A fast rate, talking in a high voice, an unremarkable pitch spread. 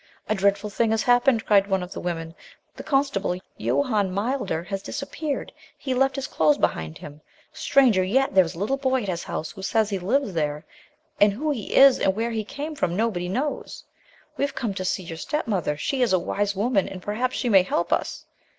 No: fast, 215 wpm; high, 205 Hz; wide, 5.8 semitones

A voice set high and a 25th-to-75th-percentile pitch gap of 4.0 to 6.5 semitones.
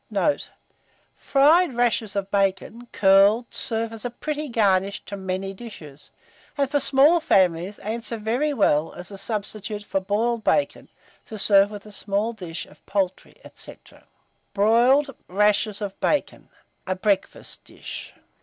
No: high, 210 Hz; average, 3.5 semitones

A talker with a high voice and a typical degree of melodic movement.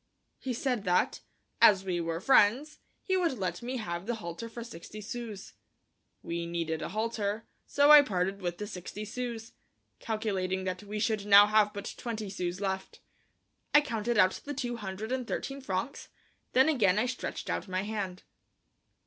Yes: high, 210 Hz; average, 4.2 semitones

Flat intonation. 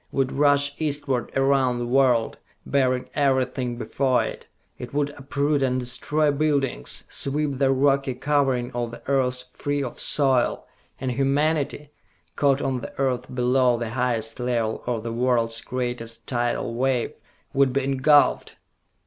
Yes: narrow, 2.3 semitones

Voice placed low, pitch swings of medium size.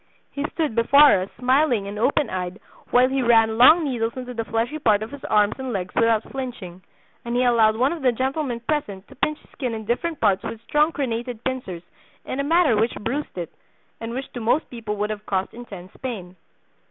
No: high, 235 Hz; average, 3.8 semitones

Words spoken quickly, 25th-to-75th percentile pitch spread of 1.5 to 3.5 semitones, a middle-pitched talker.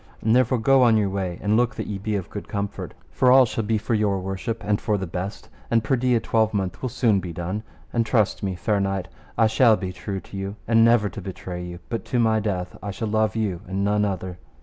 No: fast, 245 wpm; average, 2.9 semitones; low, 105 Hz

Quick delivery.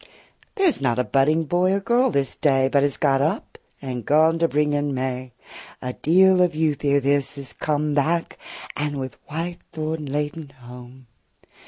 No: average, 185 wpm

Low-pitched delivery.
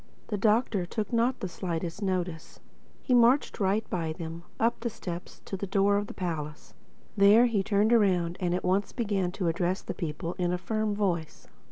No: high, 195 Hz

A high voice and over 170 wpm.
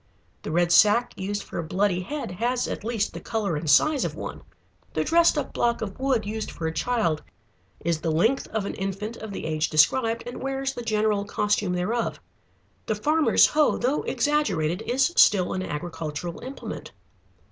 Yes: high, 210 Hz; average, 180 wpm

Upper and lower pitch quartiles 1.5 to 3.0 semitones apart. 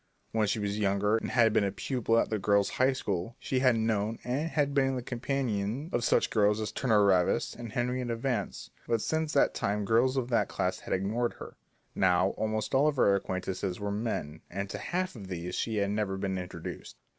No: average, 3.9 semitones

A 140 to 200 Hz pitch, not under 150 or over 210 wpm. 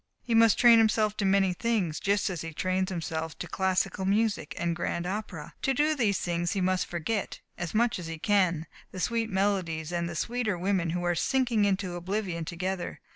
Yes: high, 190 Hz; average, 195 wpm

